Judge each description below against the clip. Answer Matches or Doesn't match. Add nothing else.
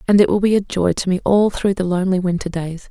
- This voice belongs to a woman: Matches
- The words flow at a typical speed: Doesn't match